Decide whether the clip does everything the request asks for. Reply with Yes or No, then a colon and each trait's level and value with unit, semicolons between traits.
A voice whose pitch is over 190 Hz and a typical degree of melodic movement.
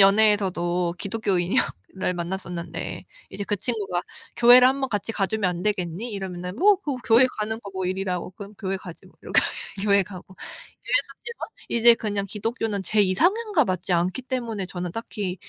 Yes: high, 200 Hz; average, 3.8 semitones